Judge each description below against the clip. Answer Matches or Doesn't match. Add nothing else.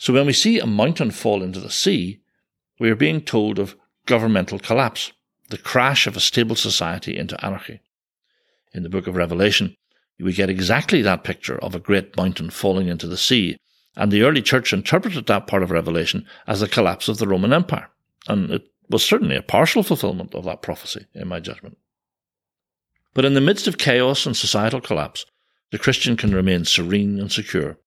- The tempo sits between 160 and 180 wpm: Doesn't match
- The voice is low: Matches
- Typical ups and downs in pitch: Matches